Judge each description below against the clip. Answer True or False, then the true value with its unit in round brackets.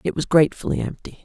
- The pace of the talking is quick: False (195 wpm)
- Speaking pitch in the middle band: True (145 Hz)